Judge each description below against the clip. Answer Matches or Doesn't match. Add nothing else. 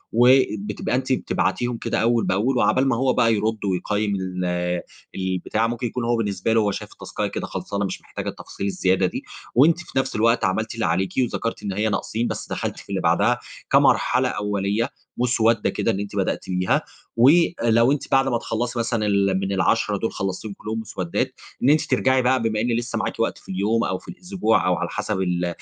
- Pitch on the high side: Doesn't match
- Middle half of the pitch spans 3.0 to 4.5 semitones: Matches